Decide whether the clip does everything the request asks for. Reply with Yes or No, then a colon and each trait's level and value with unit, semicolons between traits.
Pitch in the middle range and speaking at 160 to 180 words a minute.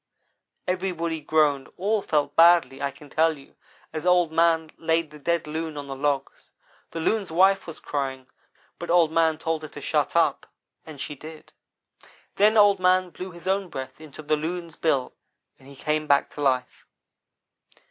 Yes: medium, 160 Hz; average, 175 wpm